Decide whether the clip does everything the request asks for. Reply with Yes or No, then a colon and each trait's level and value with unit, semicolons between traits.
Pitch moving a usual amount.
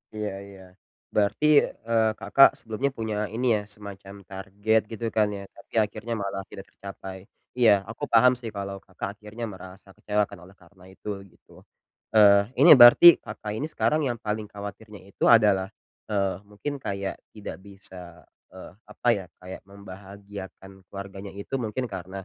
No: narrow, 2.3 semitones